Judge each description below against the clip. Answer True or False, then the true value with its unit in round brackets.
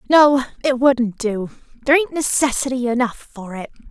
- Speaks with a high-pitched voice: True (250 Hz)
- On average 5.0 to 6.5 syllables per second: True (5.1 syllables/s)